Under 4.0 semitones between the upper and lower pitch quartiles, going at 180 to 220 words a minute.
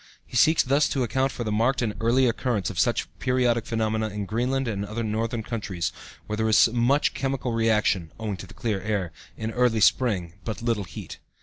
Yes: average, 2.8 semitones; average, 200 wpm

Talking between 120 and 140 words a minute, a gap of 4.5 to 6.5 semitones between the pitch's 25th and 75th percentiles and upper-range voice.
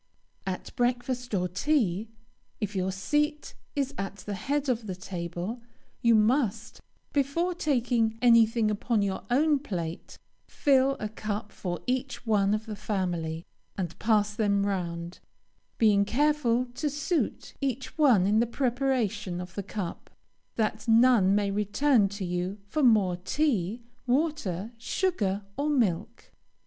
Yes: slow, 135 wpm; average, 4.9 semitones; high, 220 Hz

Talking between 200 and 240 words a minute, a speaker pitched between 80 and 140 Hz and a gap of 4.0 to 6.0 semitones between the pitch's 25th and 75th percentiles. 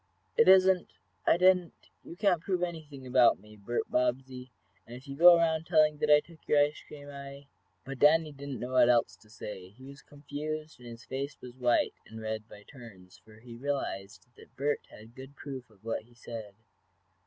Yes: fast, 205 wpm; low, 135 Hz; average, 4.4 semitones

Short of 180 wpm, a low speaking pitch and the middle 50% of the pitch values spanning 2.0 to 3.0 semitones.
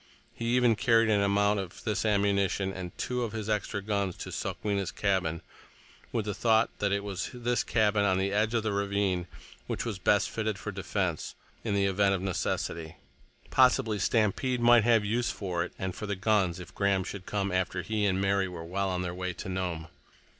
No: average, 200 wpm; low, 100 Hz; narrow, 2.6 semitones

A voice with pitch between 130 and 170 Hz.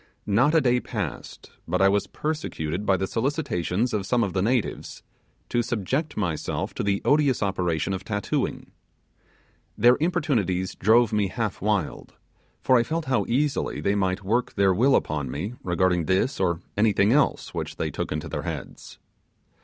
No: low, 105 Hz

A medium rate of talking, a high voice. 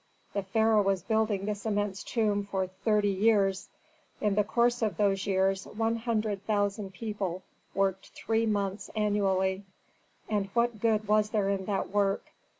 Yes: average, 150 wpm; high, 205 Hz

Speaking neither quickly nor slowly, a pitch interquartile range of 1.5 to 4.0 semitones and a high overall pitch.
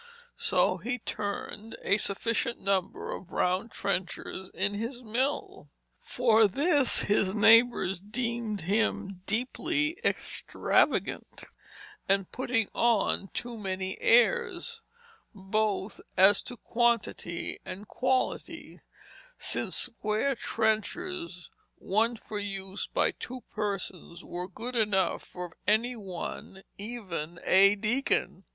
No: slow, 105 wpm; average, 3.7 semitones; high, 215 Hz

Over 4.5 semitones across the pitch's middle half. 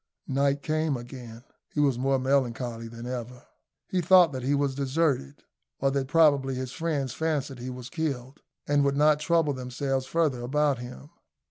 No: average, 2.9 semitones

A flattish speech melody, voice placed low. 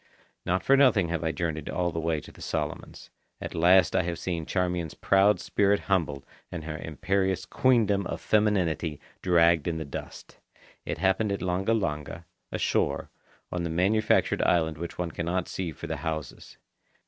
No: average, 3.0 semitones; very low, 90 Hz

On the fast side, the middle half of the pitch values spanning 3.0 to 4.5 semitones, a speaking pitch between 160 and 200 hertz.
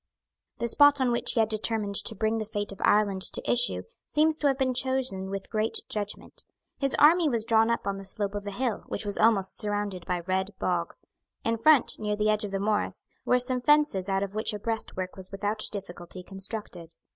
No: fast, 215 wpm; average, 3.3 semitones; high, 210 Hz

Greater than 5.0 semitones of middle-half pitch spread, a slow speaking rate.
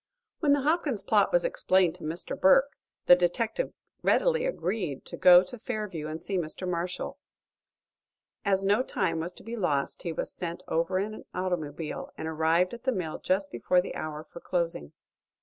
No: wide, 5.4 semitones; average, 180 wpm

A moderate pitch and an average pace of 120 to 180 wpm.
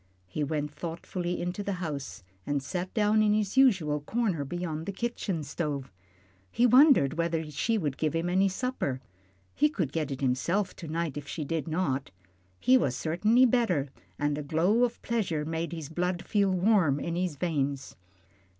Yes: medium, 170 Hz; average, 175 wpm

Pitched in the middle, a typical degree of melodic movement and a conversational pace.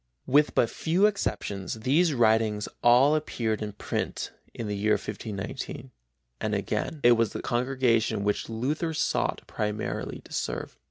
No: low, 115 Hz; average, 4.6 semitones; average, 145 wpm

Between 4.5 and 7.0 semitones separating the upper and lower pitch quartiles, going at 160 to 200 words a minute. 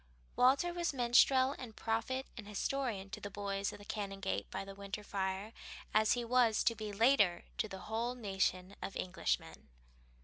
No: average, 3.8 semitones; average, 170 wpm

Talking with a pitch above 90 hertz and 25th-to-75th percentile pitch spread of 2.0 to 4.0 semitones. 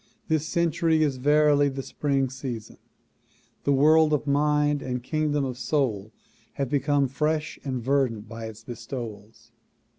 Yes: medium, 140 Hz; average, 3.3 semitones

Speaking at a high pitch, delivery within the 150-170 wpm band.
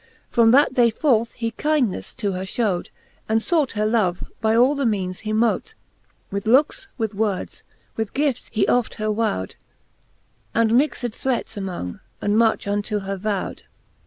Yes: high, 220 Hz; average, 160 wpm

